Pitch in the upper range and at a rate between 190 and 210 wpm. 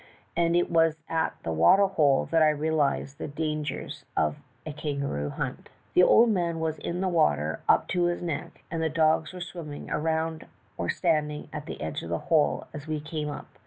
No: medium, 155 Hz; average, 200 wpm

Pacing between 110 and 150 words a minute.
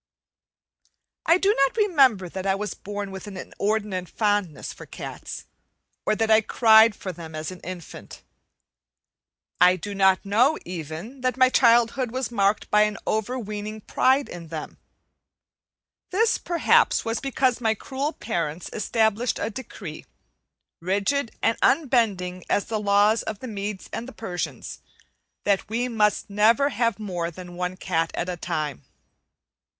Yes: average, 145 wpm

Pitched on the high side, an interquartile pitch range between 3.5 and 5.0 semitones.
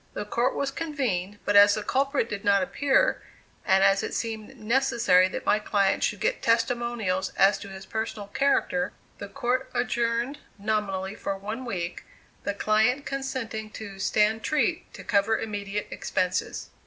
Yes: high, 215 Hz; average, 3.8 semitones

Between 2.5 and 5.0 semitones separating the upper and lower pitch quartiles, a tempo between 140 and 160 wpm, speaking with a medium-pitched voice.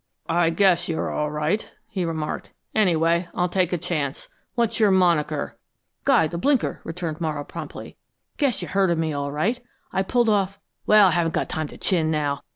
No: average, 3.9 semitones; average, 185 wpm; medium, 170 Hz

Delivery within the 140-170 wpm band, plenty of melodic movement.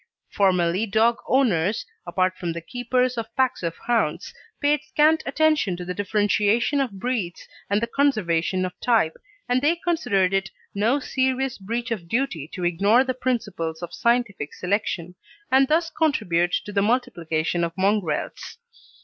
Yes: average, 150 wpm; wide, 6.1 semitones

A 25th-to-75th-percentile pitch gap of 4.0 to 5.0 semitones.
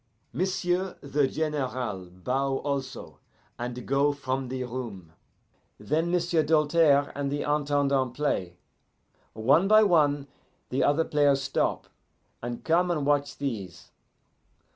No: average, 3.0 semitones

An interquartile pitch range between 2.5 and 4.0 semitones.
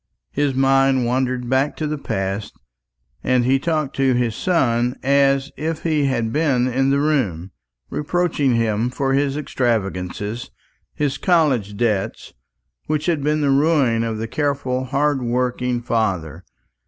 Yes: average, 3.5 semitones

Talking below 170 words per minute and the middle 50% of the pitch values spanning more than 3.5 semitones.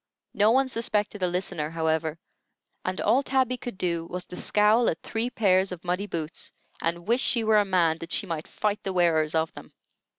No: average, 200 wpm; average, 4.5 semitones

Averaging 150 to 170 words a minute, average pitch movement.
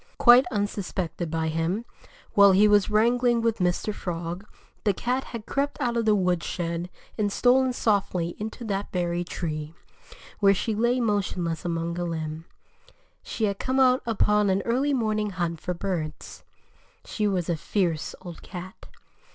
Yes: average, 155 wpm; average, 4.6 semitones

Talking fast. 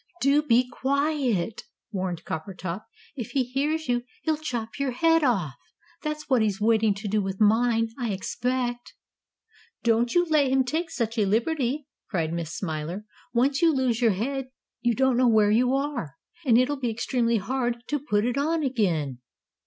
No: average, 170 wpm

